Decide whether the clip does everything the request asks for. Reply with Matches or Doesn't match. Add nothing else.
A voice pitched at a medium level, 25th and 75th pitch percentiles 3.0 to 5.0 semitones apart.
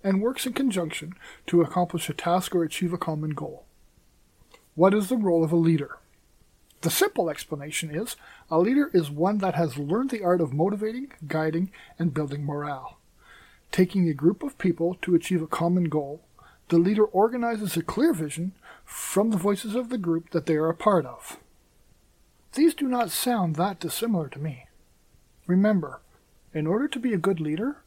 Matches